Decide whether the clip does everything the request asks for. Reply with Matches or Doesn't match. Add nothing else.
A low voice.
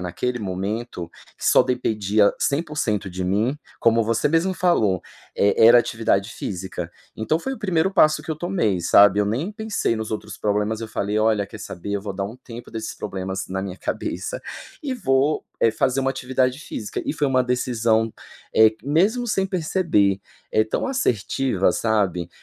Matches